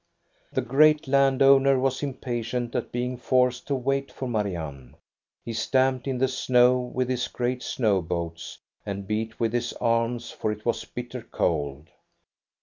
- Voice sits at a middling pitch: No, low, 125 Hz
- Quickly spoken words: No, average, 155 wpm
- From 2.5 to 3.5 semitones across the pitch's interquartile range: Yes, average, 3.0 semitones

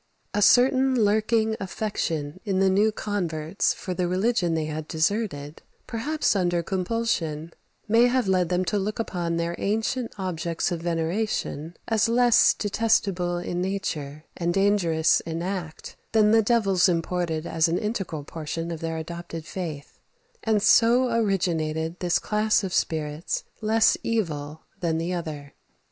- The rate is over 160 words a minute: No, average, 145 wpm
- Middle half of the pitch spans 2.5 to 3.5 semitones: No, average, 4.7 semitones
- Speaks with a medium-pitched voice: Yes, medium, 180 Hz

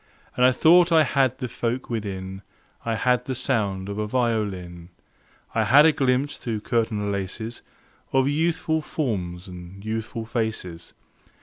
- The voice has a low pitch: Yes, low, 115 Hz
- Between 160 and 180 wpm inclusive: No, average, 145 wpm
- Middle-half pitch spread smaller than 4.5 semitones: No, average, 4.8 semitones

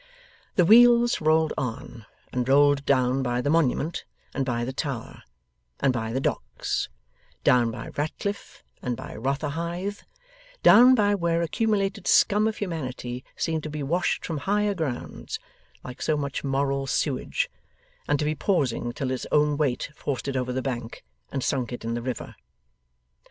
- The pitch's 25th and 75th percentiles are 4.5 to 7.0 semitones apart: Yes, average, 5.0 semitones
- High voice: No, medium, 140 Hz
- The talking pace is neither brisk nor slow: Yes, average, 160 wpm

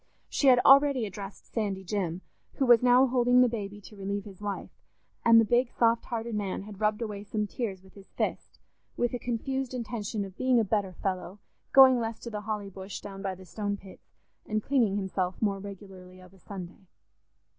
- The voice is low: No, high, 210 Hz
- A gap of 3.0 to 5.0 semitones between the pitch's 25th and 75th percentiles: Yes, average, 3.4 semitones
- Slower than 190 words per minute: No, average, 200 wpm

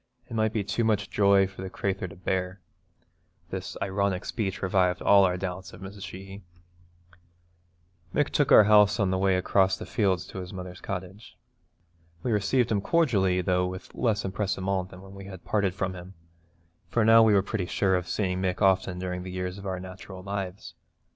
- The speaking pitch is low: Yes, very low, 95 Hz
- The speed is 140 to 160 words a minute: No, average, 190 wpm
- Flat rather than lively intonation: Yes, narrow, 1.7 semitones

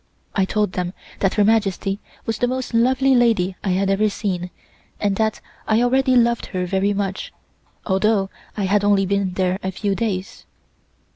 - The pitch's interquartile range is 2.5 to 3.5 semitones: Yes, average, 2.9 semitones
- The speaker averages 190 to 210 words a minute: No, average, 170 wpm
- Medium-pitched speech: No, high, 200 Hz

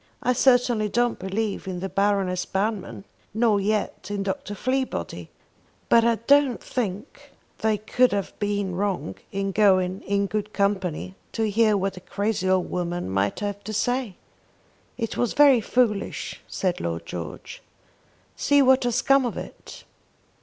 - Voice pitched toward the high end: Yes, high, 205 Hz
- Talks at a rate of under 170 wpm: Yes, average, 150 wpm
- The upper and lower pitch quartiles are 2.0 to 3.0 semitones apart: No, average, 3.6 semitones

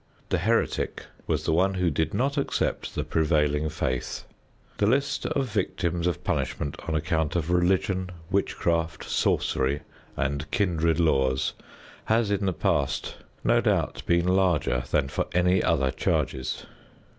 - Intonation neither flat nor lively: Yes, average, 4.2 semitones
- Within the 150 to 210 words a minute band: No, average, 140 wpm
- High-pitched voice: No, very low, 85 Hz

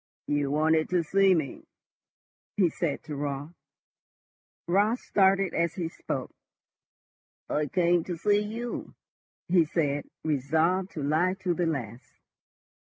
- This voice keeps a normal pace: No, slow, 125 wpm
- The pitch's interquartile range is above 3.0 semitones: Yes, average, 3.9 semitones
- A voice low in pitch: No, medium, 165 Hz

